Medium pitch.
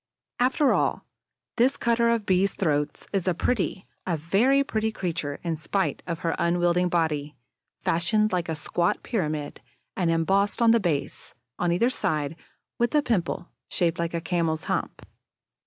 Yes: medium, 175 Hz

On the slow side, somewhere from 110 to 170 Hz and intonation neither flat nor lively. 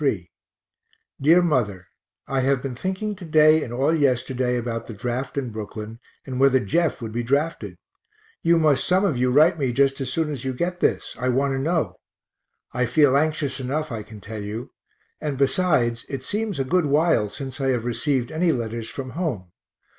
No: average, 190 wpm; low, 135 Hz; average, 4.4 semitones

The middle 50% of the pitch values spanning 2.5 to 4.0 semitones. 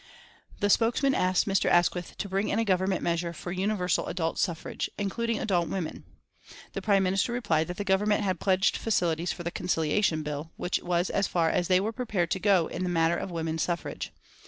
Yes: average, 2.9 semitones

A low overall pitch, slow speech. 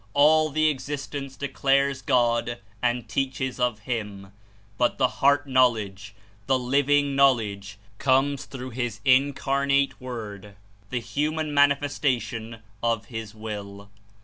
Yes: low, 130 Hz; slow, 115 wpm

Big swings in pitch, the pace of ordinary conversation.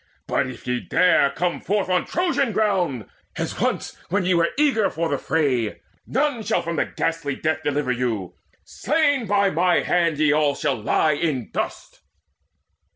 Yes: wide, 6.1 semitones; average, 160 wpm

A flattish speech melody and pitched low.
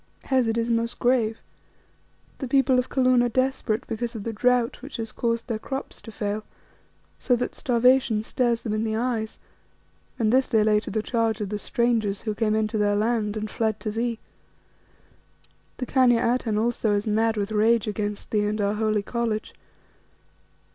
No: narrow, 2.1 semitones; high, 225 Hz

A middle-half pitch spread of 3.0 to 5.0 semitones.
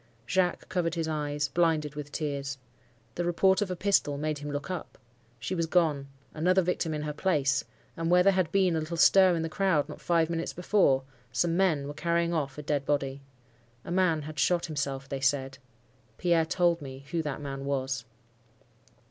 Yes: average, 3.6 semitones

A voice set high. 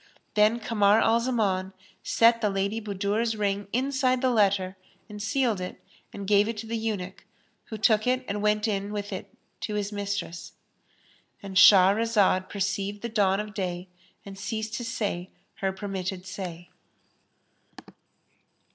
Yes: high, 205 Hz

